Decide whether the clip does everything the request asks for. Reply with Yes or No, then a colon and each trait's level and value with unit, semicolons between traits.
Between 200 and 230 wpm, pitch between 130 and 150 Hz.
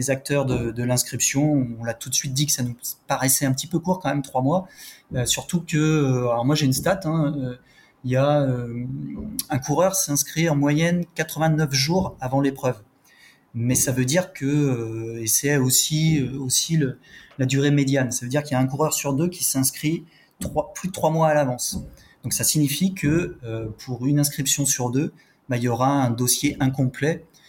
Yes: average, 210 wpm; medium, 140 Hz